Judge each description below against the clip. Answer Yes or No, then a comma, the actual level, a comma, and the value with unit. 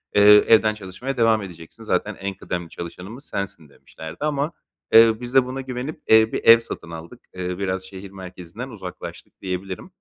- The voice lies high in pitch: No, low, 100 Hz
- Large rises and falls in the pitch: No, average, 4.0 semitones